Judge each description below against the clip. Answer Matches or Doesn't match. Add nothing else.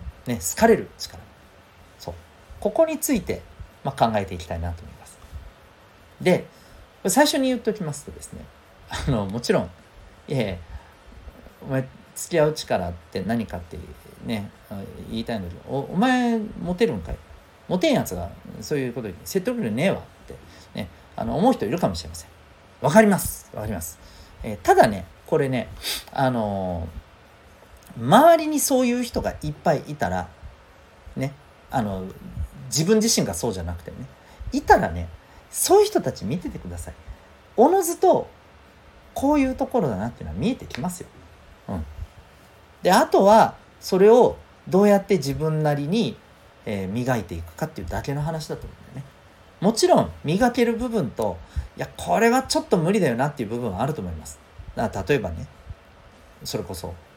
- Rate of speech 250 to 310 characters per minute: Doesn't match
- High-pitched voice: Doesn't match